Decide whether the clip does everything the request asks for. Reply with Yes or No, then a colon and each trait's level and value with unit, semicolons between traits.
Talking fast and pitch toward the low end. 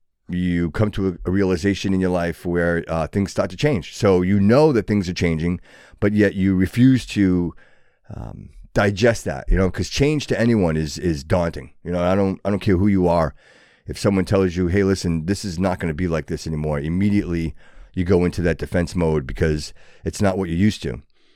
Yes: fast, 215 wpm; very low, 90 Hz